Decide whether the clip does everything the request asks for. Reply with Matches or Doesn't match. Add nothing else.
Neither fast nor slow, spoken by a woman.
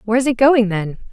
Doesn't match